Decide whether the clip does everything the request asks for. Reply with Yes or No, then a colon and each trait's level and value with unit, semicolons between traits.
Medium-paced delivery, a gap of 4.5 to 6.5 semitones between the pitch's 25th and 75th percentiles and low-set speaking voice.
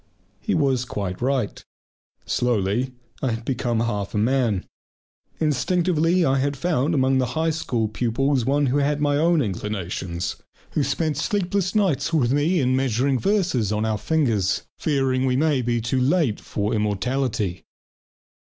Yes: average, 150 wpm; average, 4.8 semitones; low, 130 Hz